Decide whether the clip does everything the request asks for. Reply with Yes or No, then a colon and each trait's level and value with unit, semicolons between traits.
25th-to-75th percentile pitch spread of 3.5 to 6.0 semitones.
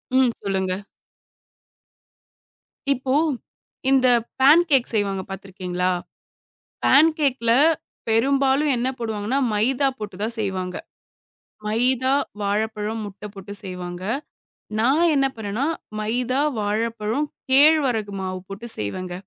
Yes: average, 4.9 semitones